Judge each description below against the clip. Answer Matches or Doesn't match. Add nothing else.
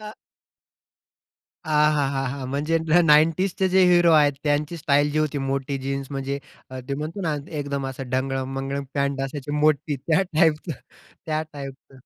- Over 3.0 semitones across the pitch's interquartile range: Doesn't match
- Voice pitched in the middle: Matches